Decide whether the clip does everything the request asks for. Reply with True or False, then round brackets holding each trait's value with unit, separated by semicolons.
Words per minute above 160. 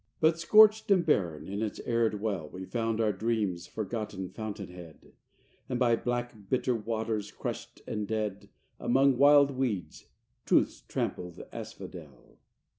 False (140 wpm)